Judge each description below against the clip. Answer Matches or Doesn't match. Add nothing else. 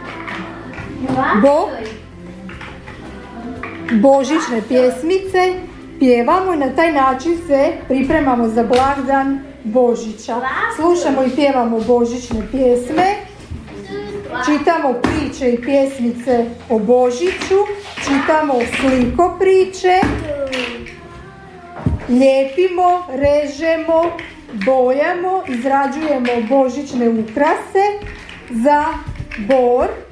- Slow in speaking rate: Matches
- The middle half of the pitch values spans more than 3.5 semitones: Matches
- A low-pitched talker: Doesn't match